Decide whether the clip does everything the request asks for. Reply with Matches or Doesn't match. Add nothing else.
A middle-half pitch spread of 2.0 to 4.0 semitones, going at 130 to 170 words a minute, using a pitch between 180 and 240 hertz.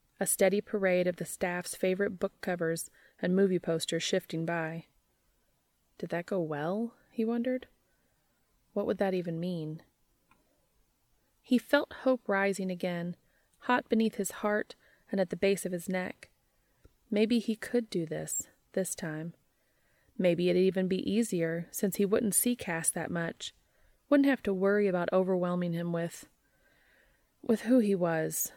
Matches